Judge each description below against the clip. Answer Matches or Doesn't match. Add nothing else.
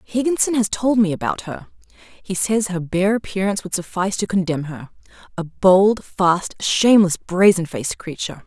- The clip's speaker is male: Doesn't match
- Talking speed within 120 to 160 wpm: Matches